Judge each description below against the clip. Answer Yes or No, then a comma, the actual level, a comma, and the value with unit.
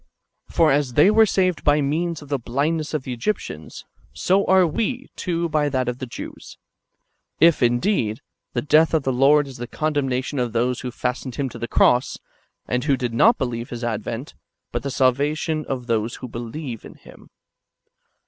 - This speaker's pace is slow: No, average, 185 wpm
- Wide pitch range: No, average, 4.2 semitones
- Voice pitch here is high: No, low, 135 Hz